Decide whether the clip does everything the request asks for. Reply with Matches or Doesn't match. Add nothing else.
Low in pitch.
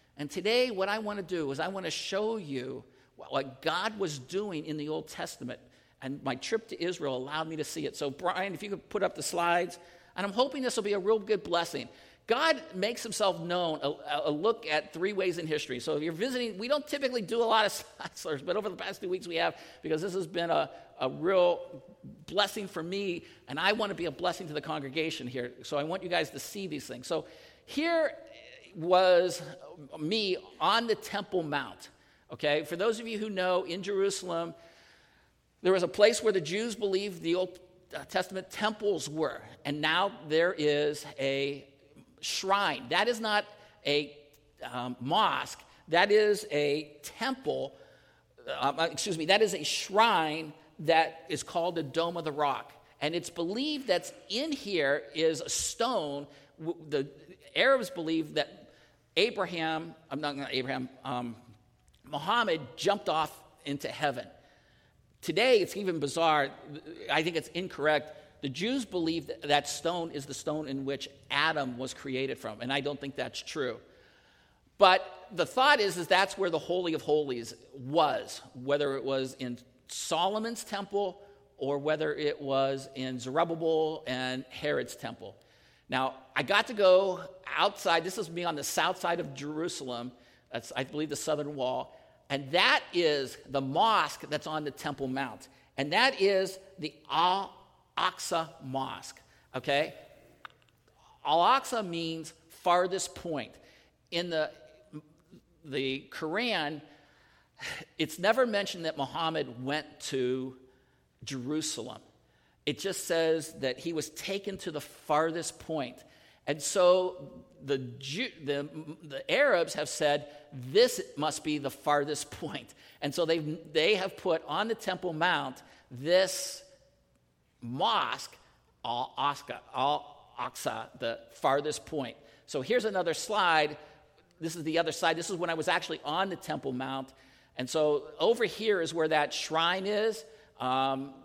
Doesn't match